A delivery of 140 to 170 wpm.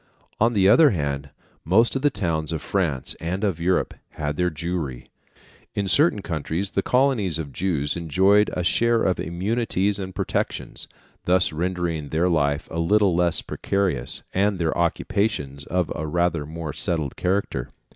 Yes: average, 155 wpm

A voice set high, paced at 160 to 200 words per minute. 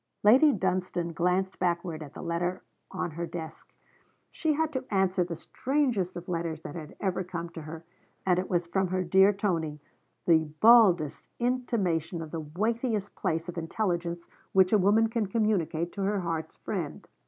No: medium, 180 Hz; average, 170 wpm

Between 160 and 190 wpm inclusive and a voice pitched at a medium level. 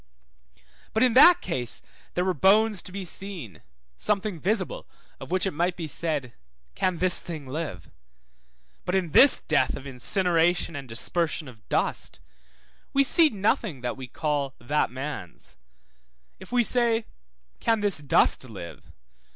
No: average, 145 wpm; medium, 175 Hz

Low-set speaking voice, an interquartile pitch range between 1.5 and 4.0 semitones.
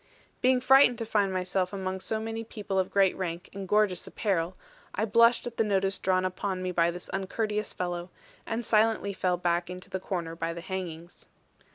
No: high, 190 Hz; average, 2.9 semitones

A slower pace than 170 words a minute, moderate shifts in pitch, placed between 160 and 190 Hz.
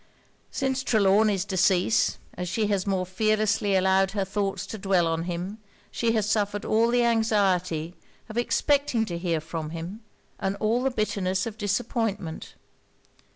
No: average, 150 wpm; average, 3.2 semitones; high, 200 Hz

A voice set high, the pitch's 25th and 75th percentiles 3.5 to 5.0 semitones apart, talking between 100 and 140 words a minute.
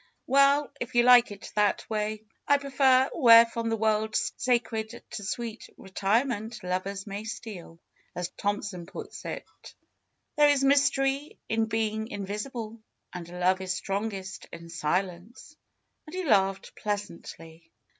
Yes: high, 215 Hz; average, 4.0 semitones; slow, 135 wpm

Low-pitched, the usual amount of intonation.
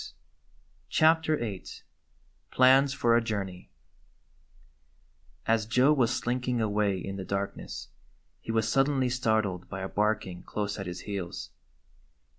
Yes: low, 110 Hz; average, 4.2 semitones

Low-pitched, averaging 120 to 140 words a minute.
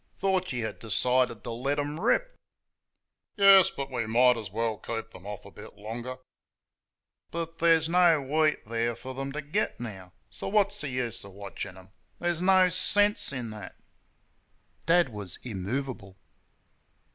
No: low, 130 Hz; average, 155 wpm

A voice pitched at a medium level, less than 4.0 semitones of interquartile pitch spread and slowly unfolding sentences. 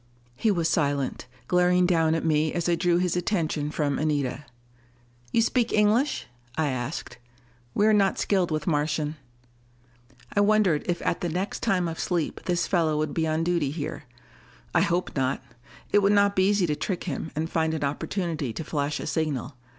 No: medium, 165 Hz; average, 3.3 semitones; average, 180 wpm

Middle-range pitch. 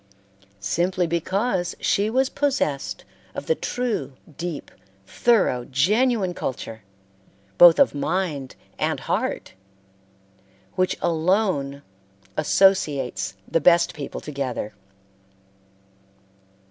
Yes: medium, 170 Hz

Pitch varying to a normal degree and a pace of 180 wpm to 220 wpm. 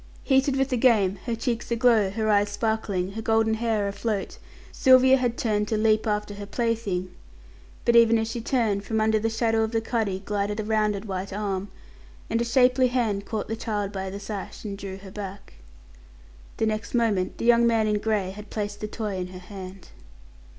No: narrow, 2.3 semitones; average, 200 wpm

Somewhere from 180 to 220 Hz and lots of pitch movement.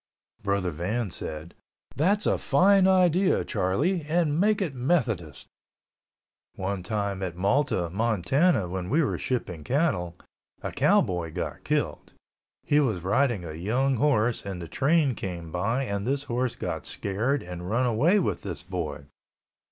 No: low, 110 Hz; wide, 8.2 semitones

